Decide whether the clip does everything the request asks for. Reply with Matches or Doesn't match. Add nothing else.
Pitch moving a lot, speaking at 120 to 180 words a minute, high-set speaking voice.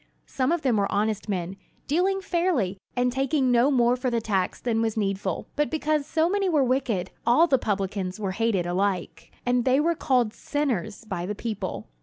Doesn't match